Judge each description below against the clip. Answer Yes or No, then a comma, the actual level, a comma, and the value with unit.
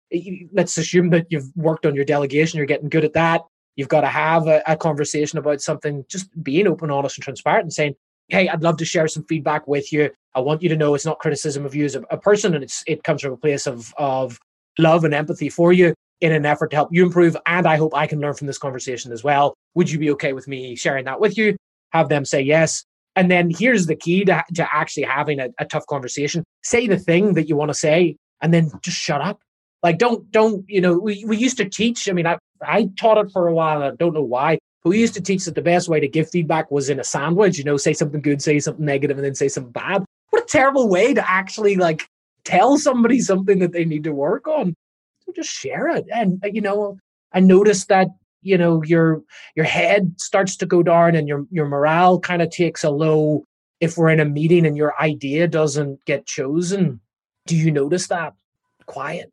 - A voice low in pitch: No, medium, 160 Hz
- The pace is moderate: No, fast, 240 wpm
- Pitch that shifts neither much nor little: Yes, average, 3.4 semitones